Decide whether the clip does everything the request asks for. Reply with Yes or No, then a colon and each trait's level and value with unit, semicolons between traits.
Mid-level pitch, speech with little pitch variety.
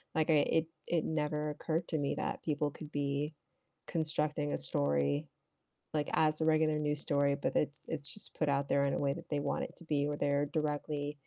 Yes: medium, 150 Hz; narrow, 1.5 semitones